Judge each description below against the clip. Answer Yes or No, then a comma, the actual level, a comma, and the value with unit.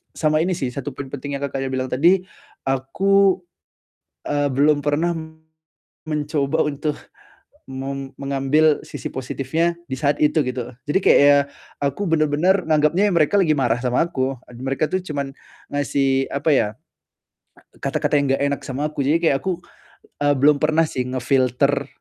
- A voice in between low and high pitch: Yes, medium, 145 Hz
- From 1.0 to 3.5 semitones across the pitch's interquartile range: Yes, narrow, 2.5 semitones